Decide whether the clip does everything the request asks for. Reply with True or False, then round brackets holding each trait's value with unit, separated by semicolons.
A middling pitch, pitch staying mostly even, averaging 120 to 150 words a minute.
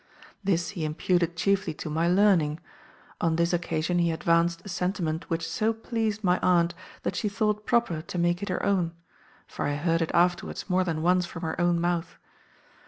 False (175 Hz; 2.2 semitones; 185 wpm)